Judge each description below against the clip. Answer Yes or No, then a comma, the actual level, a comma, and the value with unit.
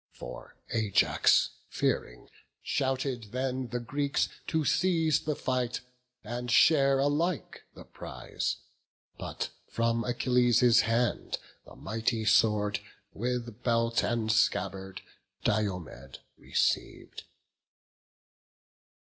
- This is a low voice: Yes, low, 120 Hz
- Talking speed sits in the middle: No, slow, 90 wpm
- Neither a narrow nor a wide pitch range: Yes, average, 3.1 semitones